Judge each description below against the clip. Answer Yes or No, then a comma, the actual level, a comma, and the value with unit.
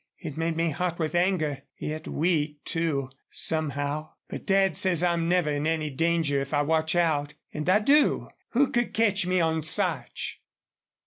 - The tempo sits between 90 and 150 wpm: No, average, 170 wpm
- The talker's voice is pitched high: No, medium, 160 Hz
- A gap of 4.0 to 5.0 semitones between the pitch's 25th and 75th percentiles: No, average, 3.0 semitones